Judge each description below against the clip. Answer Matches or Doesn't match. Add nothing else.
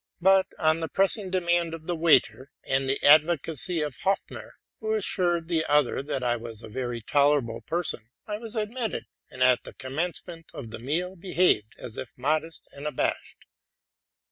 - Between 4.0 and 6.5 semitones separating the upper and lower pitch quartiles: Matches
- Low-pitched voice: Doesn't match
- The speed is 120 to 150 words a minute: Doesn't match